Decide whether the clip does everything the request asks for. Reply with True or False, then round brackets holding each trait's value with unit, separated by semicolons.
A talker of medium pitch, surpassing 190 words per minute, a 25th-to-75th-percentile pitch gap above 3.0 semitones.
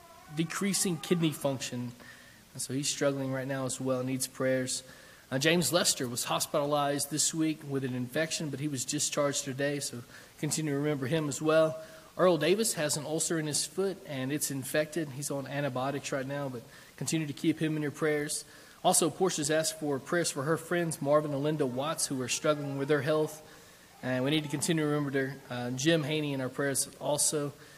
False (150 Hz; 200 wpm; 2.6 semitones)